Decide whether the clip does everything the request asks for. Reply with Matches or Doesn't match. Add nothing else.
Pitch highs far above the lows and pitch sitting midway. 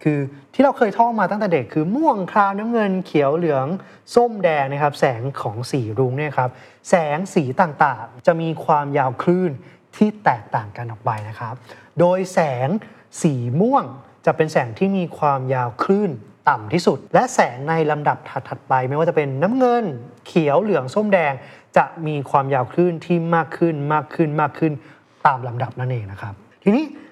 Matches